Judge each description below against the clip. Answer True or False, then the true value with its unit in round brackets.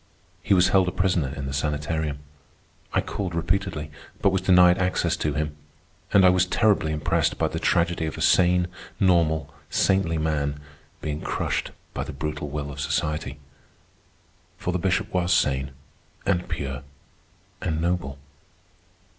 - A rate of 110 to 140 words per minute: False (150 wpm)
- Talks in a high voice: False (85 Hz)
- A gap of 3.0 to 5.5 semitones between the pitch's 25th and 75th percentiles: True (3.5 semitones)